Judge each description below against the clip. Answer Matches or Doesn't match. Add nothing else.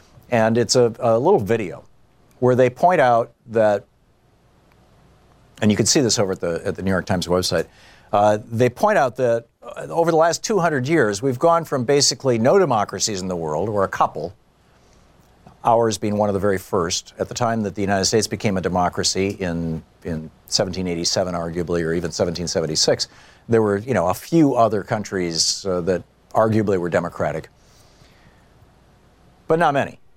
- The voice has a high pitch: Doesn't match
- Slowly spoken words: Doesn't match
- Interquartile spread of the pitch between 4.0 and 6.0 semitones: Matches